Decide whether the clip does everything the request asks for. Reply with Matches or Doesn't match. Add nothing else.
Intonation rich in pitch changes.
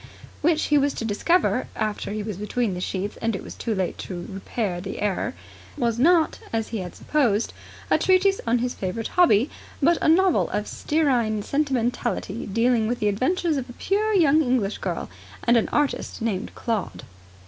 Matches